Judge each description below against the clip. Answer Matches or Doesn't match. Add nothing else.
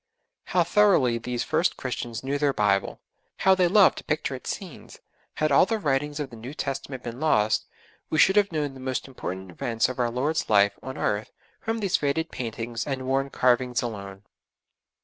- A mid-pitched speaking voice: Doesn't match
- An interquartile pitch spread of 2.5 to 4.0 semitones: Doesn't match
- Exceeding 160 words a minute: Matches